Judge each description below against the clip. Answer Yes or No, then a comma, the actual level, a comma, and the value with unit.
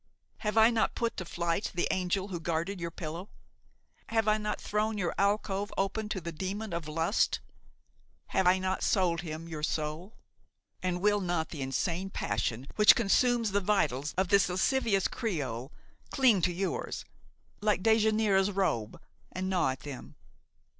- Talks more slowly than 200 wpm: Yes, average, 160 wpm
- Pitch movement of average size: Yes, average, 4.0 semitones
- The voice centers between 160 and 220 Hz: Yes, high, 190 Hz